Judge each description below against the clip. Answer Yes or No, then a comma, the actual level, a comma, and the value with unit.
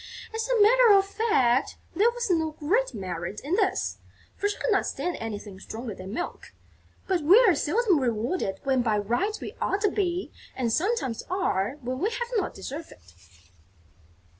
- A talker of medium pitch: No, very high, 330 Hz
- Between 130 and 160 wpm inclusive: No, average, 175 wpm